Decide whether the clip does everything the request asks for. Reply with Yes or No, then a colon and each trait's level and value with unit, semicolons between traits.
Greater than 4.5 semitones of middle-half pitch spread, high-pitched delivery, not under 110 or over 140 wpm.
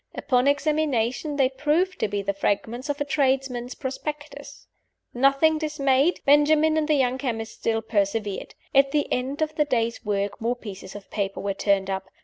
No: average, 5.0 semitones; very high, 260 Hz; average, 170 wpm